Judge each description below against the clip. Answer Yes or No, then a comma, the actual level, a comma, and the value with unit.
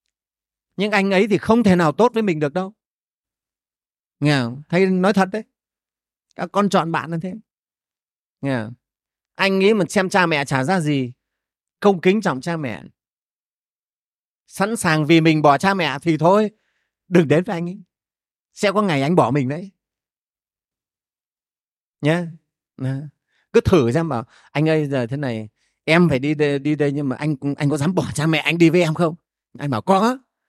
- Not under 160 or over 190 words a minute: Yes, average, 185 wpm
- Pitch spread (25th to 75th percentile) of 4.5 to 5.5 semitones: Yes, average, 4.9 semitones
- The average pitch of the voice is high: No, medium, 165 Hz